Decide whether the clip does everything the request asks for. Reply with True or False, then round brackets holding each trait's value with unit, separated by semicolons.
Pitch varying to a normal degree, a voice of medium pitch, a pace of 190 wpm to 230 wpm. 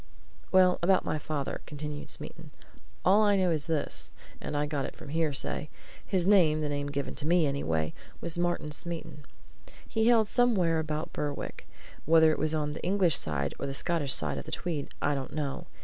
True (3.4 semitones; 155 Hz; 195 wpm)